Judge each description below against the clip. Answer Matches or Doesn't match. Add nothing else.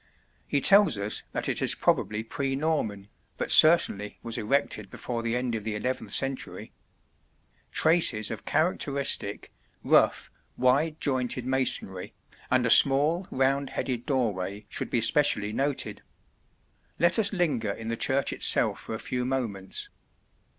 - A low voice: Matches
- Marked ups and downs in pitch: Doesn't match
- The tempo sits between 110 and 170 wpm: Matches